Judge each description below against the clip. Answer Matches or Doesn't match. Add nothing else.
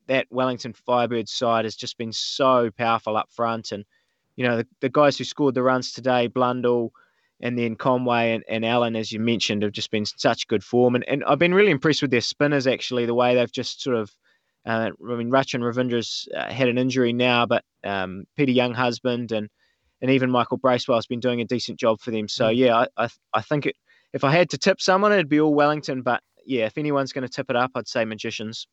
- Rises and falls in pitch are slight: Matches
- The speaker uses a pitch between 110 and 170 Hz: Matches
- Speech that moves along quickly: Matches